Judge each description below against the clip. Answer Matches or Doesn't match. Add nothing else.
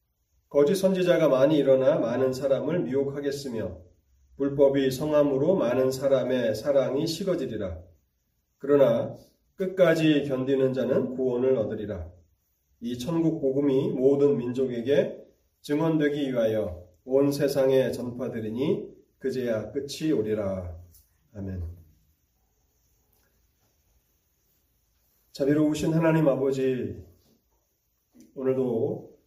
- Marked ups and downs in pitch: Matches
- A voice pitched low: Matches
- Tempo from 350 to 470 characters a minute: Doesn't match